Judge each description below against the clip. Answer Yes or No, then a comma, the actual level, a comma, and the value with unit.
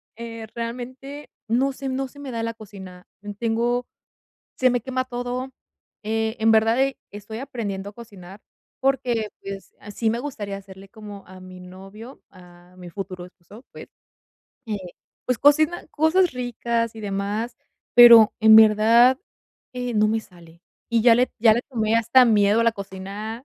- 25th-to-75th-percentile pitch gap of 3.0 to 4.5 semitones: Yes, average, 3.5 semitones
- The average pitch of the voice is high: Yes, high, 225 Hz